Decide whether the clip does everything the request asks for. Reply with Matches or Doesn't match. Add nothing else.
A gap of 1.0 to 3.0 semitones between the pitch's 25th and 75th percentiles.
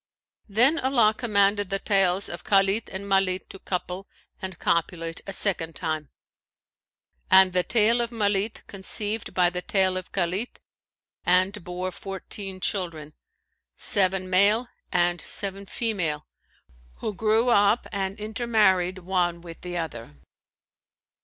Matches